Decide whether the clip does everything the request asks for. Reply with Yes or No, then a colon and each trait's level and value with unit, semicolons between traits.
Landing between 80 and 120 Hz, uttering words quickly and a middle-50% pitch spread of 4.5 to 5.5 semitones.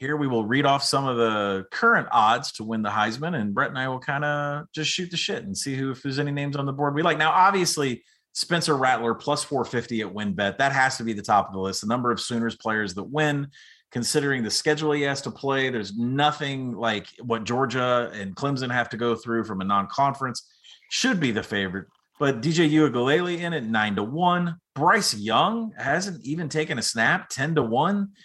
No: low, 135 Hz; fast, 225 wpm; average, 4.8 semitones